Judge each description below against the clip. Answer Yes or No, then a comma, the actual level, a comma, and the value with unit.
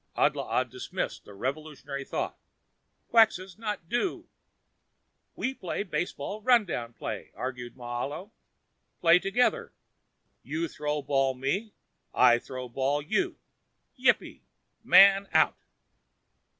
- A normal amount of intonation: No, wide, 7.4 semitones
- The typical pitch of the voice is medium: Yes, medium, 155 Hz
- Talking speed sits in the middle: No, slow, 105 wpm